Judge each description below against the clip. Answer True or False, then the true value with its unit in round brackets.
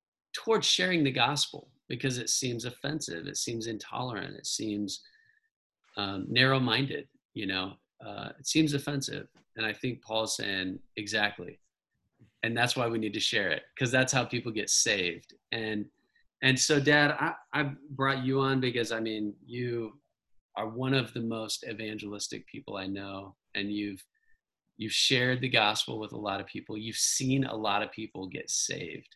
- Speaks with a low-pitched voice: True (120 Hz)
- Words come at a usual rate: True (170 wpm)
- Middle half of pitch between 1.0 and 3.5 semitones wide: False (4.2 semitones)